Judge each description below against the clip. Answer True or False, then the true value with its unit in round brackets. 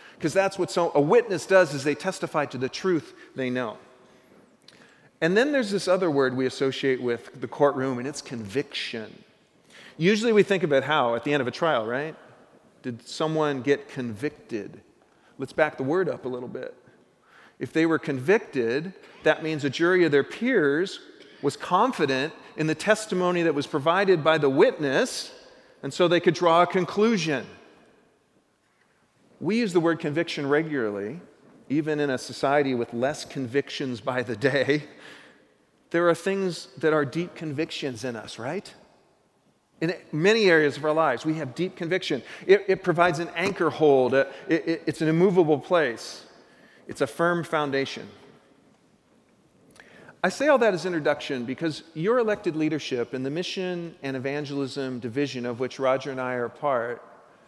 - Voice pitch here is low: False (155 Hz)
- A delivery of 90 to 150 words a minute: False (165 wpm)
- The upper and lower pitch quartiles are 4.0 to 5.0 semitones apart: True (4.6 semitones)